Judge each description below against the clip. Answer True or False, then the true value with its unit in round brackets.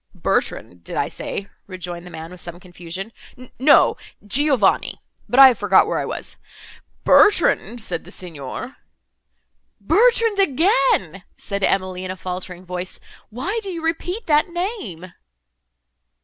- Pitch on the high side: True (200 Hz)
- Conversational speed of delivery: False (130 wpm)